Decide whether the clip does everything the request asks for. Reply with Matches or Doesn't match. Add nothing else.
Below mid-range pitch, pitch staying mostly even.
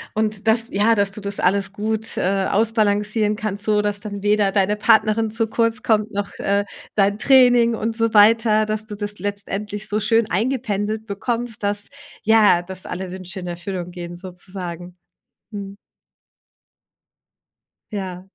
Doesn't match